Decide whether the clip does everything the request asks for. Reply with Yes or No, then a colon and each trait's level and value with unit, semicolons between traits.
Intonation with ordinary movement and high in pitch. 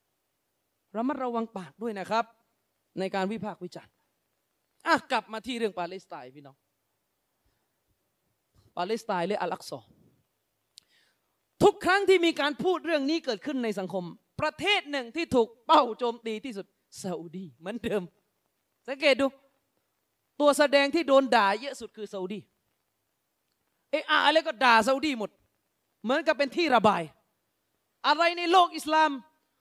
No: wide, 6.7 semitones; high, 240 Hz